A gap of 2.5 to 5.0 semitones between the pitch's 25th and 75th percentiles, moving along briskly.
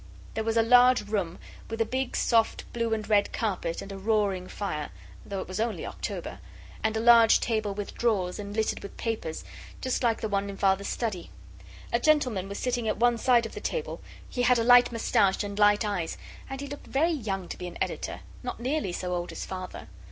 Yes: average, 3.4 semitones; fast, 215 wpm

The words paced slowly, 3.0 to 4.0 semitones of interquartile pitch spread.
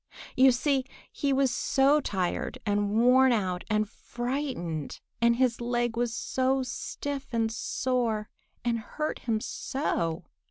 Yes: slow, 130 wpm; average, 3.4 semitones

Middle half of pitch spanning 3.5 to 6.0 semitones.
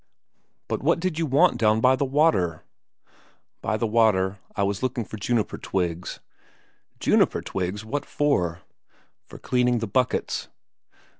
Yes: average, 5.3 semitones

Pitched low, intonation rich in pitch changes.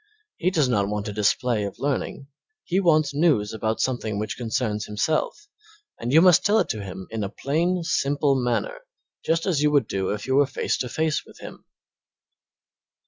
Yes: low, 130 Hz; wide, 6.8 semitones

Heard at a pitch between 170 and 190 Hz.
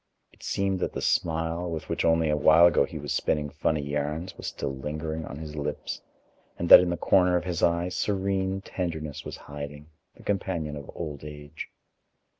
No: very low, 80 Hz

